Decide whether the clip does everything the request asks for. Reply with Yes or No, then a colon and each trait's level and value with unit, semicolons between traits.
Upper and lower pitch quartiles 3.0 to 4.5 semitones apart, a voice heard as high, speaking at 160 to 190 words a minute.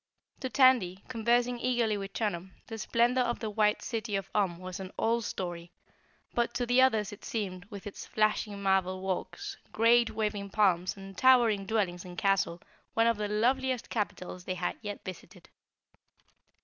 Yes: average, 3.6 semitones; high, 210 Hz; average, 165 wpm